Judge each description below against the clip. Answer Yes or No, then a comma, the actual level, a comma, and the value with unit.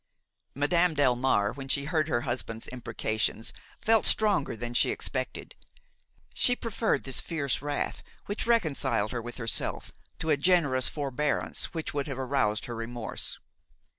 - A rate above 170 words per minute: No, average, 140 wpm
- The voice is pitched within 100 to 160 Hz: Yes, medium, 140 Hz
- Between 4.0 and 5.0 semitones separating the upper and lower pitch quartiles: Yes, average, 4.7 semitones